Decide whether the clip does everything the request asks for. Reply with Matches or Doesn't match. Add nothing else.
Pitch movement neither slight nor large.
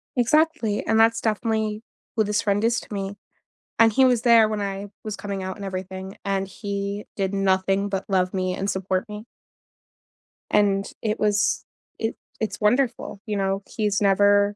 Doesn't match